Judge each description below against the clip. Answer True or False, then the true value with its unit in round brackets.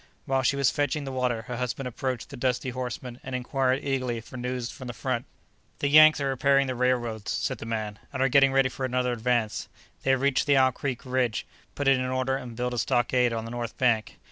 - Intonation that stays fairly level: True (1.7 semitones)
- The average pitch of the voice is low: True (125 Hz)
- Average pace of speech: False (230 wpm)